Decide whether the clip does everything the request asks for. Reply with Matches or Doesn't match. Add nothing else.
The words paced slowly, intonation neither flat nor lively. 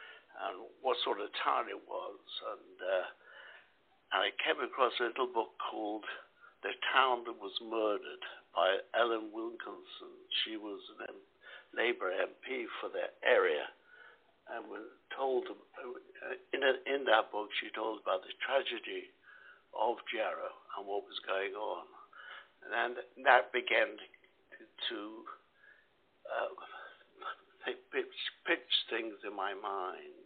Matches